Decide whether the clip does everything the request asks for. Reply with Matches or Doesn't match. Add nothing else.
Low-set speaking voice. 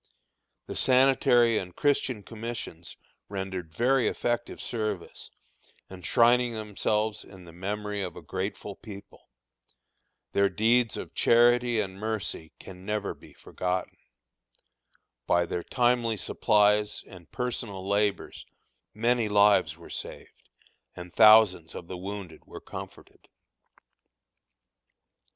Matches